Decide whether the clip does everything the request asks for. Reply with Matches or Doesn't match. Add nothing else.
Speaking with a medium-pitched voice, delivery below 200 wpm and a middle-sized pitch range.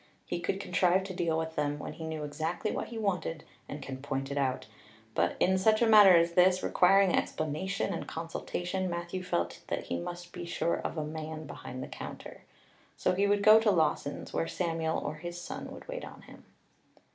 Doesn't match